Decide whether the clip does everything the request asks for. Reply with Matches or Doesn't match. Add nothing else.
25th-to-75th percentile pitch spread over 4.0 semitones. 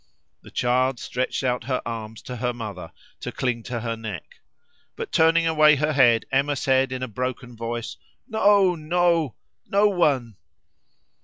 Matches